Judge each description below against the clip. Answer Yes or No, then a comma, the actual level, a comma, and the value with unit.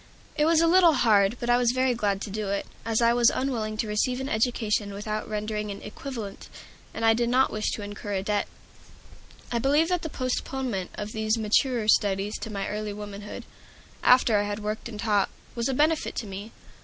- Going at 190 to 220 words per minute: Yes, fast, 205 wpm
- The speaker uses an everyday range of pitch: Yes, average, 3.1 semitones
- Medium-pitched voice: No, high, 220 Hz